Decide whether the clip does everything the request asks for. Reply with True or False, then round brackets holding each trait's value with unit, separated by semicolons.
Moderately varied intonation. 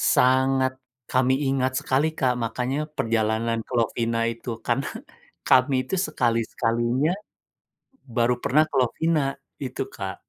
False (2.3 semitones)